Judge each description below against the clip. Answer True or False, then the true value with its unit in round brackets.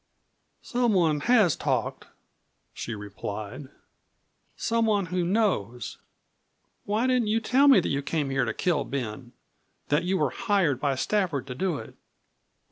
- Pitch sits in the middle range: True (170 Hz)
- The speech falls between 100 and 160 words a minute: True (135 wpm)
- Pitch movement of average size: False (8.2 semitones)